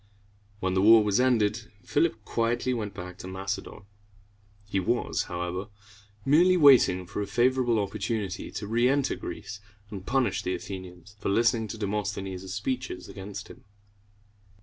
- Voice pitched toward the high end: No, low, 105 Hz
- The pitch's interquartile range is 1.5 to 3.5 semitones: No, average, 4.0 semitones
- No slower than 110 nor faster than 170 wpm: Yes, average, 140 wpm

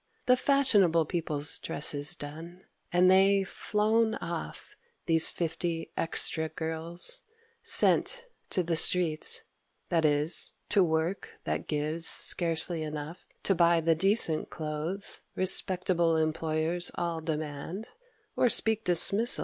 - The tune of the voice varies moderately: Yes, average, 3.1 semitones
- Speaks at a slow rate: Yes, slow, 110 wpm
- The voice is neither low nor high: Yes, medium, 170 Hz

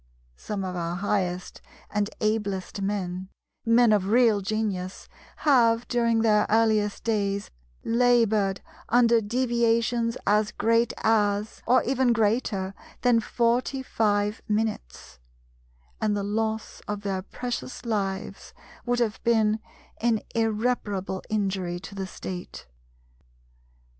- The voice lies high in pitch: Yes, high, 215 Hz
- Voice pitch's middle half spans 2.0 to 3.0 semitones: Yes, narrow, 2.6 semitones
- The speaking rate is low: Yes, slow, 115 wpm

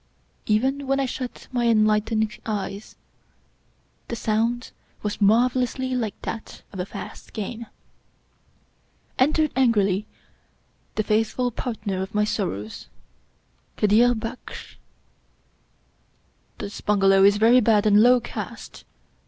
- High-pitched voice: Yes, high, 220 Hz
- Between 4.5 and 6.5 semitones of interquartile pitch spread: No, average, 2.8 semitones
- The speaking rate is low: Yes, slow, 110 wpm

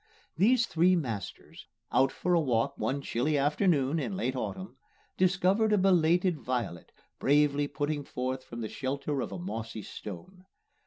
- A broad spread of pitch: Yes, wide, 5.8 semitones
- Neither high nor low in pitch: Yes, medium, 145 Hz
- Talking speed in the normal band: Yes, average, 150 wpm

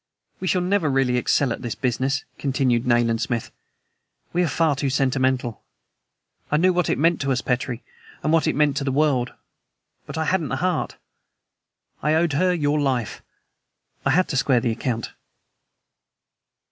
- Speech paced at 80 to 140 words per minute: No, average, 165 wpm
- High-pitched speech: No, medium, 140 Hz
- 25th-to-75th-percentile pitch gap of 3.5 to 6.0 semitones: Yes, average, 4.2 semitones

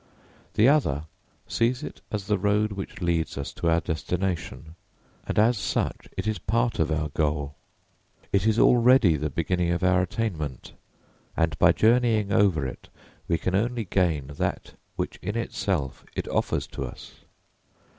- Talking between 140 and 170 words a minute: Yes, average, 155 wpm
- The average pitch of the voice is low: Yes, very low, 90 Hz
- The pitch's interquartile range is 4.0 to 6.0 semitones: Yes, average, 5.2 semitones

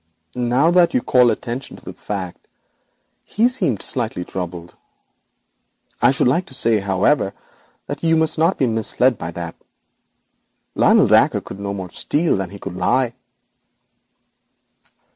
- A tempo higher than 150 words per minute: No, average, 145 wpm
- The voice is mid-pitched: No, low, 120 Hz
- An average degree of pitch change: No, wide, 7.2 semitones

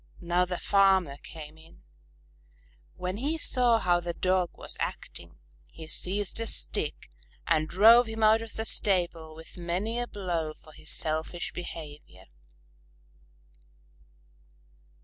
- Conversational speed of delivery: No, slow, 130 wpm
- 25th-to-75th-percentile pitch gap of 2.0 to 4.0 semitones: No, average, 4.8 semitones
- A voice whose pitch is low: No, medium, 180 Hz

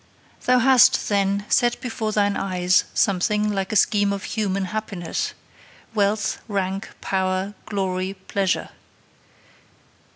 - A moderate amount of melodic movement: No, narrow, 2.0 semitones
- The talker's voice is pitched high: Yes, high, 200 Hz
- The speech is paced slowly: Yes, slow, 110 wpm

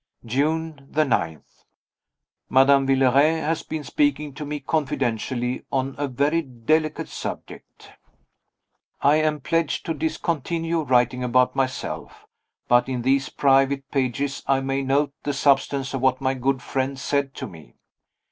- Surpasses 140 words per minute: No, slow, 135 wpm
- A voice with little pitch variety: Yes, narrow, 2.3 semitones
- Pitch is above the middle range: No, low, 135 Hz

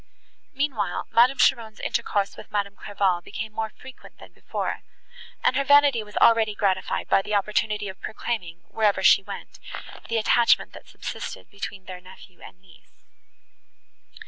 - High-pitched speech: Yes, high, 210 Hz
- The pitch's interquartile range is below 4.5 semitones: Yes, average, 2.9 semitones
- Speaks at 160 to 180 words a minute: No, average, 145 wpm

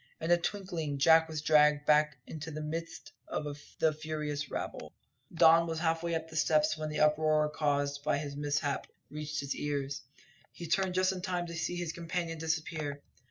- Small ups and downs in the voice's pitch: Yes, narrow, 1.8 semitones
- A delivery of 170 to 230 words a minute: Yes, average, 185 wpm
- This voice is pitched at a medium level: Yes, medium, 155 Hz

